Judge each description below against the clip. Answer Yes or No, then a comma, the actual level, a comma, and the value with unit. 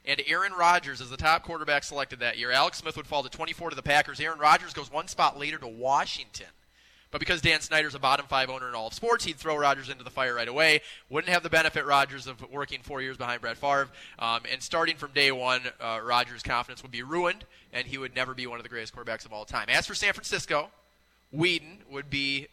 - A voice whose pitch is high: No, medium, 140 Hz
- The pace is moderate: No, fast, 240 wpm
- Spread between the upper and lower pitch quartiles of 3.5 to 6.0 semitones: Yes, average, 3.9 semitones